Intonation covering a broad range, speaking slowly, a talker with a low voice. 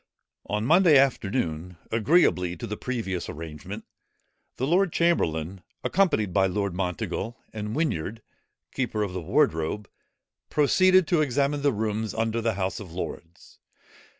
Yes: wide, 7.3 semitones; slow, 130 wpm; low, 110 Hz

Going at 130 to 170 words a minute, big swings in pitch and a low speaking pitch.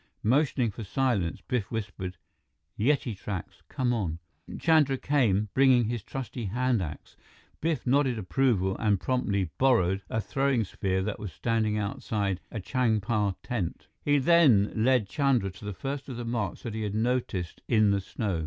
No: average, 160 wpm; average, 4.6 semitones; low, 110 Hz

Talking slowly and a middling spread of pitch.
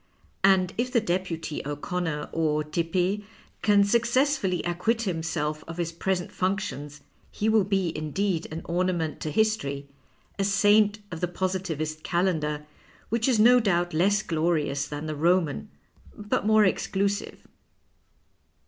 Yes: slow, 130 wpm; average, 4.4 semitones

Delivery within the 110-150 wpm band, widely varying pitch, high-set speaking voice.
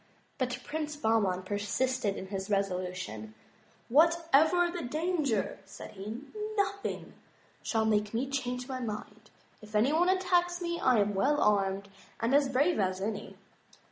Yes: average, 145 wpm; wide, 7.1 semitones; high, 240 Hz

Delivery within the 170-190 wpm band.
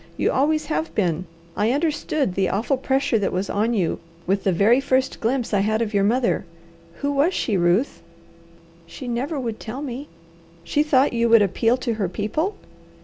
Yes: average, 185 wpm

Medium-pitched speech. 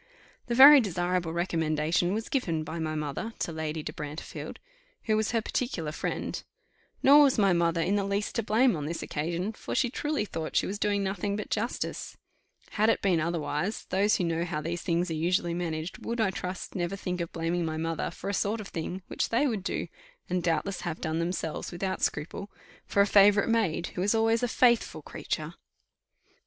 Yes: medium, 180 Hz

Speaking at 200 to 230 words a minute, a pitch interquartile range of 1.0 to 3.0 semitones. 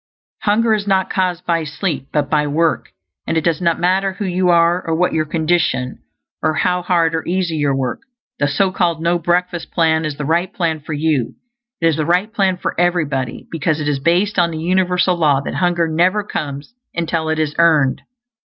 Yes: fast, 205 wpm; narrow, 2.6 semitones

